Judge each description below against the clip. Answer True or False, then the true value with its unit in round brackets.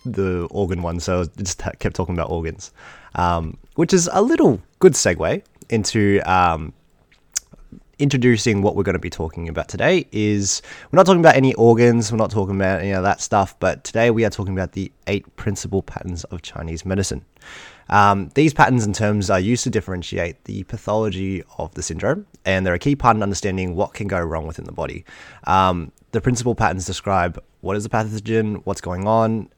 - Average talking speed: True (195 wpm)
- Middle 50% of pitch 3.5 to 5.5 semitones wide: True (3.8 semitones)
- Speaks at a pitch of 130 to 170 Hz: False (100 Hz)